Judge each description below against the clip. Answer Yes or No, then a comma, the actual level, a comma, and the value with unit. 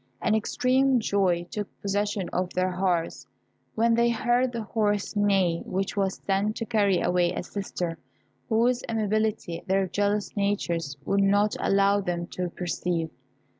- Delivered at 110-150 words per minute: Yes, average, 145 wpm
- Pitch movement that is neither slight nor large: Yes, average, 3.1 semitones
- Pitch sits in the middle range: No, high, 200 Hz